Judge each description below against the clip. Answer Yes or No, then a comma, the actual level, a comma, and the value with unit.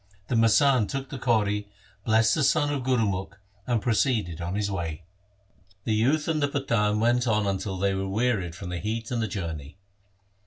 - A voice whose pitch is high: No, low, 110 Hz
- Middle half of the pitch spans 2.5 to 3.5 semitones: No, average, 4.3 semitones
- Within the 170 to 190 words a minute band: Yes, average, 185 wpm